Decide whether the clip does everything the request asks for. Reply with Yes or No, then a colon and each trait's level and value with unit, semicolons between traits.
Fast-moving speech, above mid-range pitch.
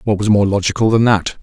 No: fast, 250 wpm; low, 105 Hz